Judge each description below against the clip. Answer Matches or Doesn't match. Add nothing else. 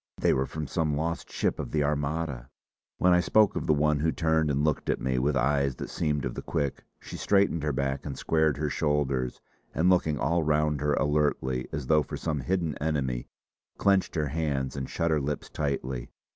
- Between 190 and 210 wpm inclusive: Matches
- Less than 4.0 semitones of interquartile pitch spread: Matches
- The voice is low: Matches